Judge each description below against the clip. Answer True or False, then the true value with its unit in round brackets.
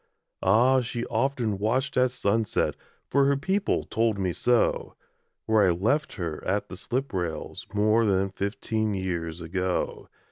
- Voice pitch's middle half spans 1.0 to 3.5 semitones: False (4.9 semitones)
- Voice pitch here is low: True (110 Hz)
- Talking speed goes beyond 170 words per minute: False (145 wpm)